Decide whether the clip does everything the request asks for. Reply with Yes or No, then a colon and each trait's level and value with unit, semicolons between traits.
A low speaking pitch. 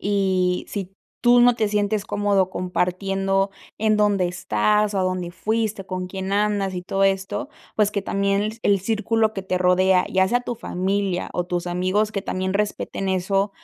No: high, 195 Hz